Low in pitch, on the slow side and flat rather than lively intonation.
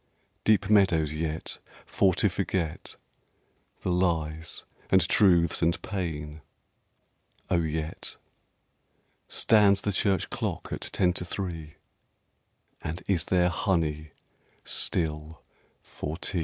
No: very low, 85 Hz; slow, 105 wpm; average, 3.2 semitones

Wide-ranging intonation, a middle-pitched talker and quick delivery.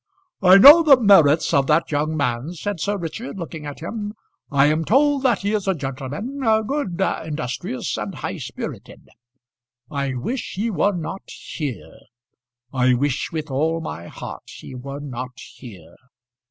No: wide, 6.8 semitones; medium, 160 Hz; average, 155 wpm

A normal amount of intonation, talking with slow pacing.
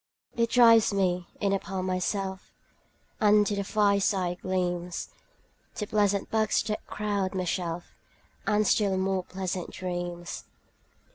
No: narrow, 2.3 semitones; slow, 130 wpm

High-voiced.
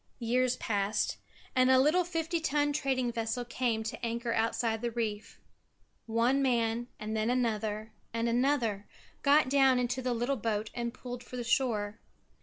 Yes: high, 240 Hz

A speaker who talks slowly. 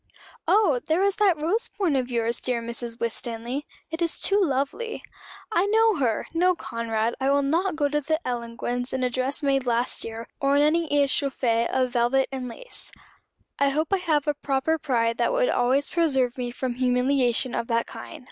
No: average, 190 wpm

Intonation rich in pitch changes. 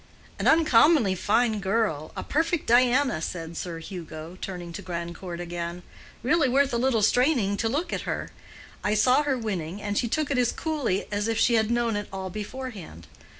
Yes: wide, 6.1 semitones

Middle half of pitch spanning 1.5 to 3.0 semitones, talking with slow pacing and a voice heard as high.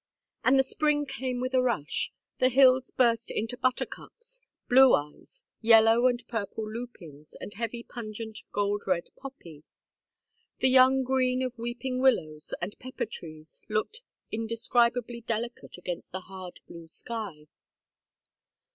No: average, 3.7 semitones; slow, 130 wpm; high, 235 Hz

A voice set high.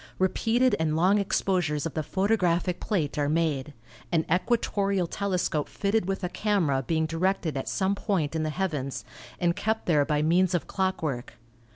No: medium, 175 Hz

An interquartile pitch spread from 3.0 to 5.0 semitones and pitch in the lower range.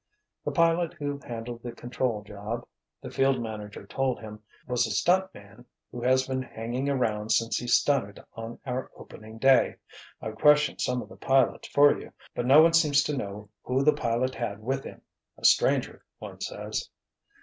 Yes: average, 3.6 semitones; low, 125 Hz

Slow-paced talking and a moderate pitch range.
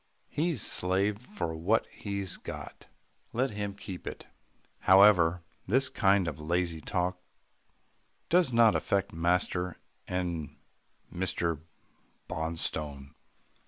Yes: slow, 100 wpm; average, 3.7 semitones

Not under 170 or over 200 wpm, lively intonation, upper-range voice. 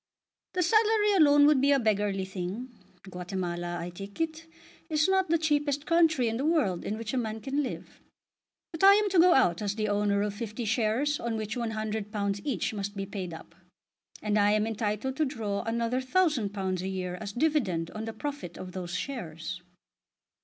Yes: average, 190 wpm; wide, 6.5 semitones; high, 220 Hz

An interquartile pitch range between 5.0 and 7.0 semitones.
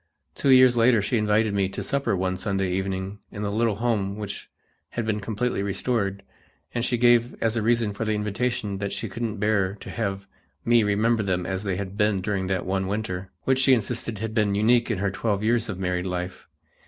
No: average, 2.9 semitones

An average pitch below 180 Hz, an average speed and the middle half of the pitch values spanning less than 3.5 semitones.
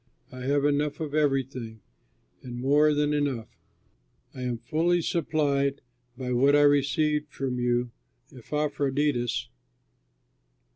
No: medium, 140 Hz; slow, 115 wpm; average, 2.9 semitones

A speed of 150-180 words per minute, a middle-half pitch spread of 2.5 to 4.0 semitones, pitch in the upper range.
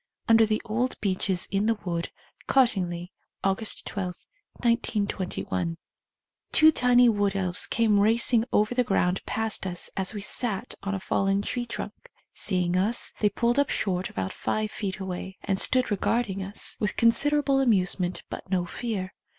Yes: average, 155 wpm; average, 3.7 semitones; high, 205 Hz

